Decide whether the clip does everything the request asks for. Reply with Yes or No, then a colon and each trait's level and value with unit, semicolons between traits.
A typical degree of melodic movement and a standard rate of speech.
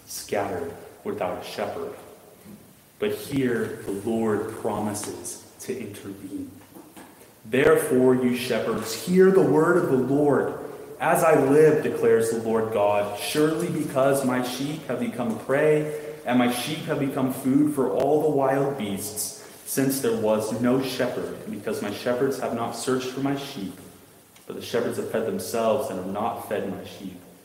Yes: average, 3.9 semitones; average, 155 wpm